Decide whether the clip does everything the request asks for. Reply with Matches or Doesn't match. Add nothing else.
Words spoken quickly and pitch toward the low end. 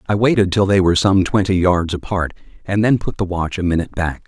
Matches